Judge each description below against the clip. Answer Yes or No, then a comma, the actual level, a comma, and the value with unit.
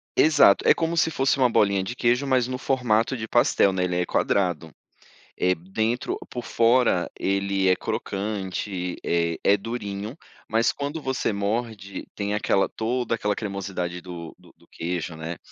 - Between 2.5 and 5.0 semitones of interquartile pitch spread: Yes, average, 4.6 semitones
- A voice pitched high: No, low, 105 Hz